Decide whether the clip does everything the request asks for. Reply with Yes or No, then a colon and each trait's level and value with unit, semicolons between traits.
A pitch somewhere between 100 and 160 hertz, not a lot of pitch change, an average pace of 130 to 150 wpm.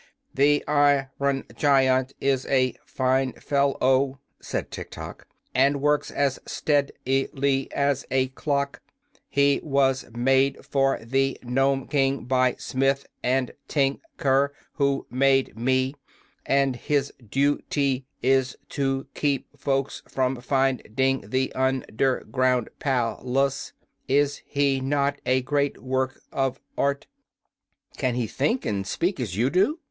Yes: low, 135 Hz; narrow, 1.3 semitones; average, 140 wpm